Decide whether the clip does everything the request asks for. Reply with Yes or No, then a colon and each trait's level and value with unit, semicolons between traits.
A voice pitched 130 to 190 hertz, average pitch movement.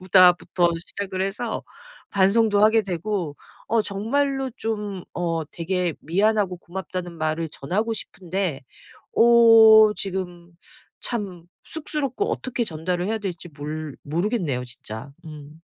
Yes: medium, 185 Hz; average, 4.6 semitones